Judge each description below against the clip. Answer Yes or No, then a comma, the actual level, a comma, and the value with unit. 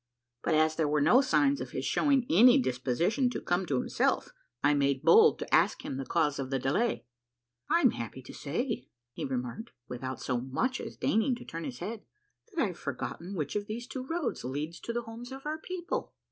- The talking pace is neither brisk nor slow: No, fast, 215 wpm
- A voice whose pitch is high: No, medium, 175 Hz